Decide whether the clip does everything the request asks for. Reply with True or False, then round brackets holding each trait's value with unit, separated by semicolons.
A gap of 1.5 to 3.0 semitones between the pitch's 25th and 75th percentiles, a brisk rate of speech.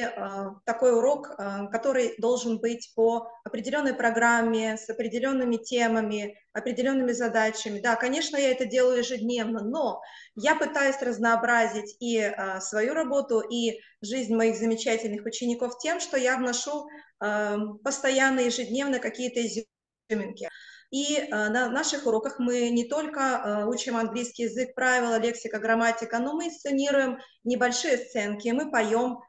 False (2.4 semitones; 120 wpm)